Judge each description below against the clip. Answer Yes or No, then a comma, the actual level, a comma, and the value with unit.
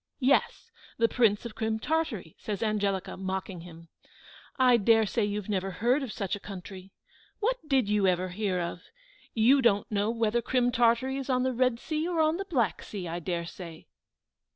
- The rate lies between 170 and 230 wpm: Yes, average, 185 wpm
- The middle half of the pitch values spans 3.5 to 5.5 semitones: Yes, average, 4.7 semitones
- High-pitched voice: Yes, high, 220 Hz